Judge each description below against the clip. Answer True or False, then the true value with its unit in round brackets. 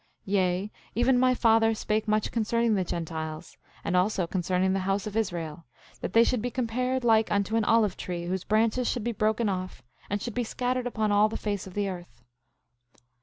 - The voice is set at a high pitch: True (210 Hz)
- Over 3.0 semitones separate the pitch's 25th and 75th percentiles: True (3.6 semitones)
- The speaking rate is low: False (200 wpm)